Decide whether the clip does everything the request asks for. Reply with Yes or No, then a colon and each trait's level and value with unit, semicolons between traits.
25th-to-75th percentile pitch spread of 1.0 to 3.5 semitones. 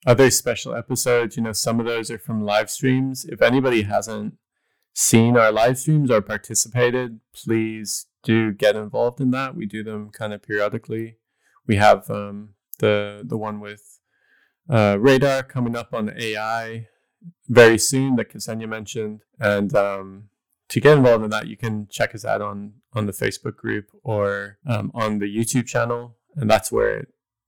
Yes: narrow, 2.6 semitones